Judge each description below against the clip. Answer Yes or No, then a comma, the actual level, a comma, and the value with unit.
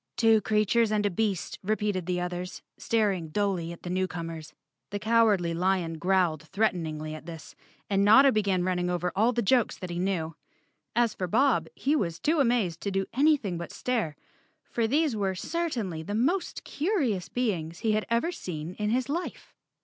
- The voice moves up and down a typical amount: Yes, average, 4.7 semitones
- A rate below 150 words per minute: No, average, 175 wpm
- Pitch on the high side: Yes, high, 195 Hz